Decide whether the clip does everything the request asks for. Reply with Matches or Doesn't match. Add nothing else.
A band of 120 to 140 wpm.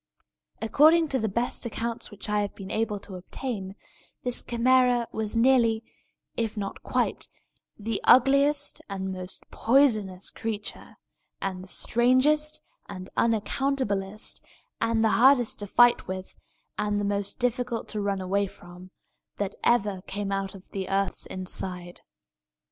Matches